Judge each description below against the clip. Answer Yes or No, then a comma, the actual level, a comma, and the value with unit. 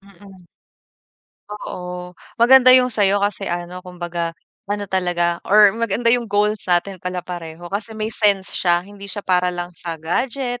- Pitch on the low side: No, high, 190 Hz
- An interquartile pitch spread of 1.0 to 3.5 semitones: Yes, average, 3.0 semitones